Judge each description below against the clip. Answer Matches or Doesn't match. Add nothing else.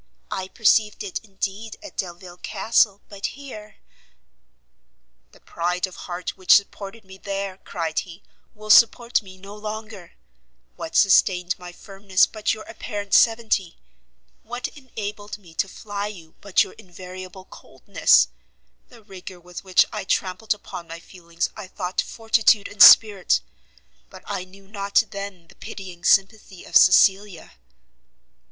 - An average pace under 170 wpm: Matches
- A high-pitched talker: Matches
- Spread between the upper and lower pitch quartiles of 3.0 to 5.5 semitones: Doesn't match